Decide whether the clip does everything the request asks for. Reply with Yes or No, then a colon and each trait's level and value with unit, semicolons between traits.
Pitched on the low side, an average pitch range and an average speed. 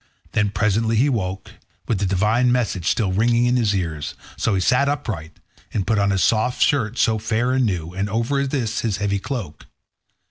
Yes: low, 110 Hz; average, 3.8 semitones; average, 190 wpm